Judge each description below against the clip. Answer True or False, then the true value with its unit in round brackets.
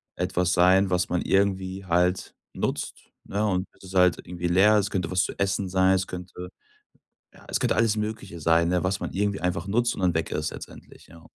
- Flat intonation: True (1.6 semitones)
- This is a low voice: True (95 Hz)